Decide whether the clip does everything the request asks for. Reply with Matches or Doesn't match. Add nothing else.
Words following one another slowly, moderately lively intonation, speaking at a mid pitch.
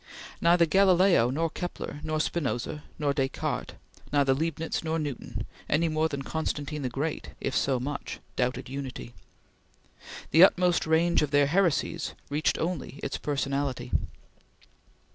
Matches